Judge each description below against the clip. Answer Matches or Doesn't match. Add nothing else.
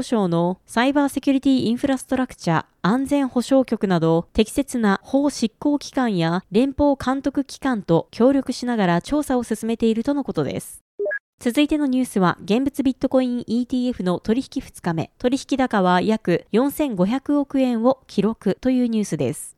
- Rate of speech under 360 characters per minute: Matches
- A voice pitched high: Matches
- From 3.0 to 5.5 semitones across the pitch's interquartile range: Matches